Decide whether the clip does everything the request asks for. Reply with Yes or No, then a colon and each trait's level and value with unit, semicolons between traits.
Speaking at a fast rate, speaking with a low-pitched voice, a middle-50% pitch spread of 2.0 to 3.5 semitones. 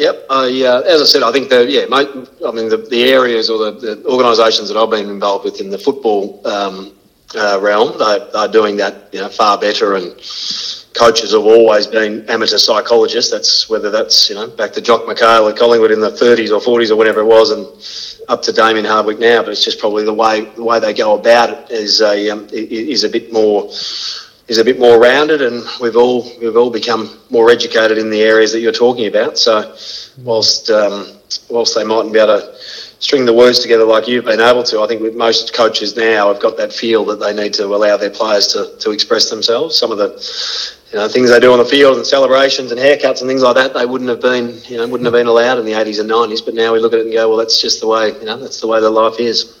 Yes: fast, 250 wpm; low, 115 Hz; average, 2.9 semitones